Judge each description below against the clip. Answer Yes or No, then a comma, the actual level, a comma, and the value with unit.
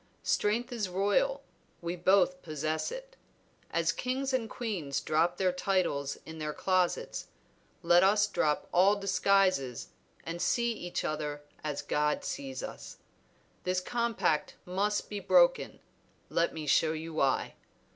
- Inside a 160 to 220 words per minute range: No, slow, 135 wpm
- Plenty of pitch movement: Yes, wide, 5.9 semitones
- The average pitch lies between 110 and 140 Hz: No, medium, 185 Hz